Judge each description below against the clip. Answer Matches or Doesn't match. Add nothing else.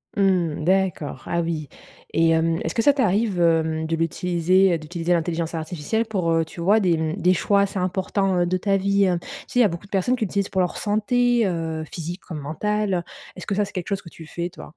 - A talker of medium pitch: Matches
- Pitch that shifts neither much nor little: Matches